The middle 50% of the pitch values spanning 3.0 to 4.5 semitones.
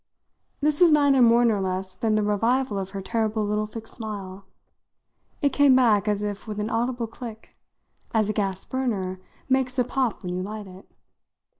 Yes: average, 3.7 semitones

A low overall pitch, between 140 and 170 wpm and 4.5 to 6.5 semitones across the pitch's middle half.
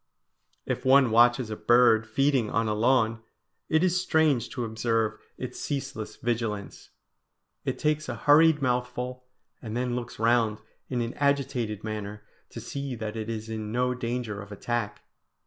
No: low, 120 Hz; average, 155 wpm; average, 2.9 semitones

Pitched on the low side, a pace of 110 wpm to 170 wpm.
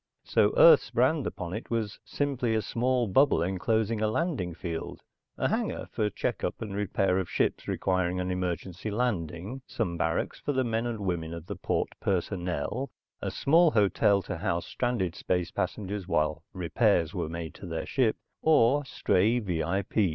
Yes: low, 100 Hz; average, 165 wpm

